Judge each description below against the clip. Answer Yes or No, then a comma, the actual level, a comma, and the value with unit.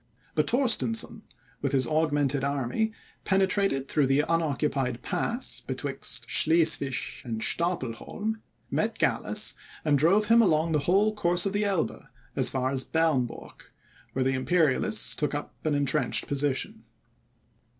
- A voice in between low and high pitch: Yes, medium, 150 Hz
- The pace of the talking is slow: Yes, slow, 130 wpm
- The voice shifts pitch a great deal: Yes, wide, 6.1 semitones